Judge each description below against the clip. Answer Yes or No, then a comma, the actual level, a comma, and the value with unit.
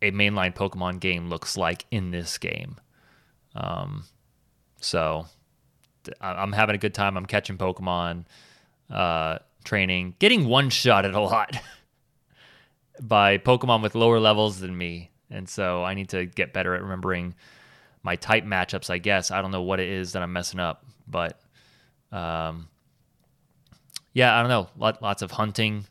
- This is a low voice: Yes, very low, 95 Hz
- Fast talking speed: No, average, 150 wpm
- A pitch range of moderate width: Yes, average, 3.0 semitones